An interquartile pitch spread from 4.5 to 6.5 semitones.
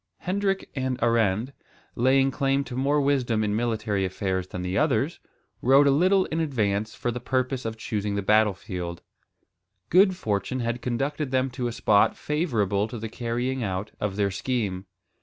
Yes: average, 4.8 semitones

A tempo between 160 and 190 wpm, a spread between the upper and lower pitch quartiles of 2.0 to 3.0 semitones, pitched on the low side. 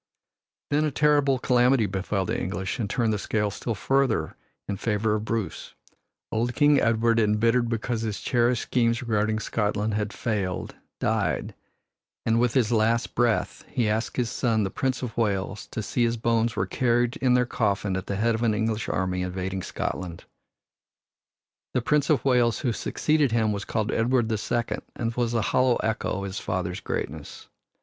Yes: average, 175 wpm; average, 2.7 semitones; low, 115 Hz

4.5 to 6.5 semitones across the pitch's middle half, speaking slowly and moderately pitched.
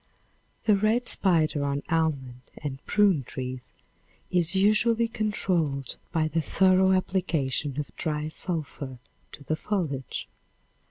Yes: average, 5.3 semitones; slow, 115 wpm; medium, 160 Hz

